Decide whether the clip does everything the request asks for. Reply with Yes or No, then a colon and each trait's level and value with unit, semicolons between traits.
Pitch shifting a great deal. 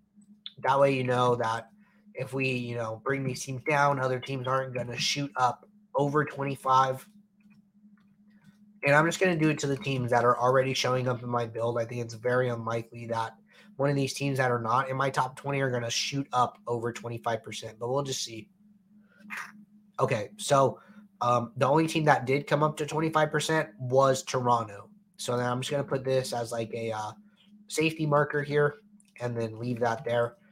No: average, 4.6 semitones